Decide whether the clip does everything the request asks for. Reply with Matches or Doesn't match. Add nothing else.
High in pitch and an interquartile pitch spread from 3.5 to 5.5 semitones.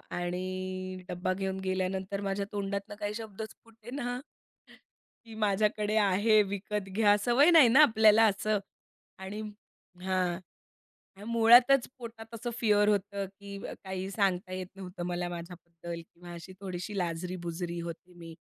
Doesn't match